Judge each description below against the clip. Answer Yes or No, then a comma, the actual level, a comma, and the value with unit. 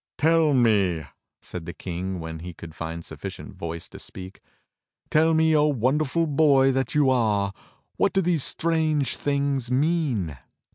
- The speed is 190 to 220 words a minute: No, average, 150 wpm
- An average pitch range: No, wide, 8.7 semitones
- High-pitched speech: No, low, 130 Hz